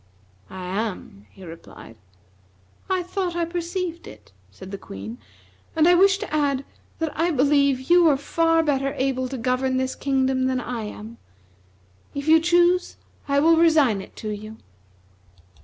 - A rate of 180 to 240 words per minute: No, average, 155 wpm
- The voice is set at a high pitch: Yes, very high, 275 Hz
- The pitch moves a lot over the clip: Yes, wide, 6.4 semitones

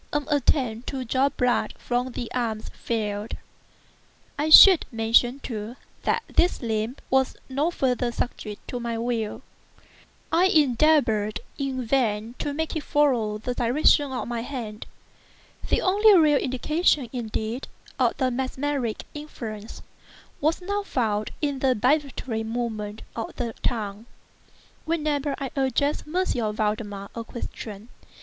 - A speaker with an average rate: No, slow, 130 wpm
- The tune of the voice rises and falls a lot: No, average, 4.5 semitones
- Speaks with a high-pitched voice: Yes, very high, 250 Hz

